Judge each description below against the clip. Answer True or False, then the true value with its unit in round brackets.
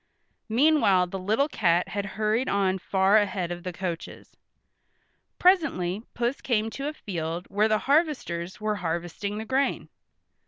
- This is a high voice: True (205 Hz)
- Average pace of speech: True (145 wpm)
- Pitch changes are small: False (4.7 semitones)